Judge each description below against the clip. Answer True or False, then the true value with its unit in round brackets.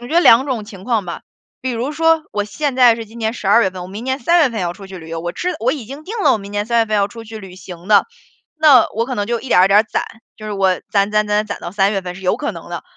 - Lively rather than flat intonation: False (4.2 semitones)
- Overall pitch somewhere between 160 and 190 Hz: False (215 Hz)